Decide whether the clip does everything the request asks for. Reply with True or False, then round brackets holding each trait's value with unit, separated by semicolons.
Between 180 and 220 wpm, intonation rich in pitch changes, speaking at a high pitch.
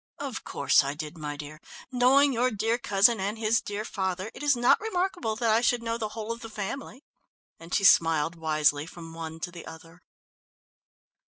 True (190 wpm; 6.1 semitones; 205 Hz)